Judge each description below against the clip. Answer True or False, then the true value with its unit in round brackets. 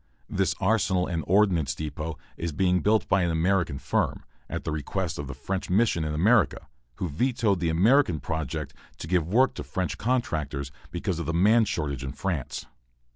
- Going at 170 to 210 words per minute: True (180 wpm)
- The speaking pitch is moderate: False (85 Hz)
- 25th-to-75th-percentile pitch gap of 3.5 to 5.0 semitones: True (4.3 semitones)